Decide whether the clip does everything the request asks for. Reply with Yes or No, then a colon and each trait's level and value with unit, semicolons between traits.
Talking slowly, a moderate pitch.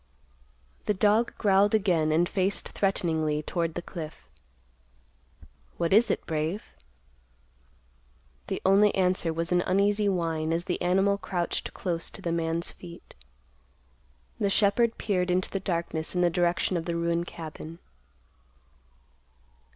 Yes: slow, 130 wpm; medium, 175 Hz